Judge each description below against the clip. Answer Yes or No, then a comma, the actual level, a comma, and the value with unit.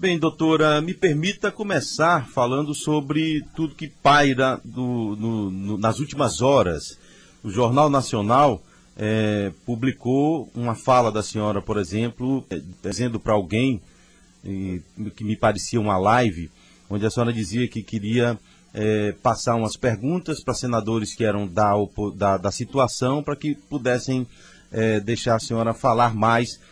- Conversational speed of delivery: Yes, average, 145 wpm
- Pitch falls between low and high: No, low, 115 Hz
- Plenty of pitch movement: No, average, 4.5 semitones